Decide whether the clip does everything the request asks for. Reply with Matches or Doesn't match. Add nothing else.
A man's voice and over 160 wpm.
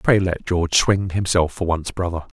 Matches